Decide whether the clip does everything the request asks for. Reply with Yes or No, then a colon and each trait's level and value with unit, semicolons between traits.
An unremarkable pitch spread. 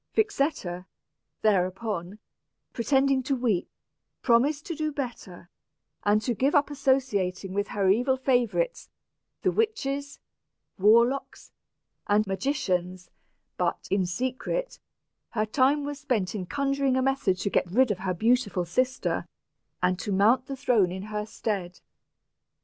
No: wide, 6.1 semitones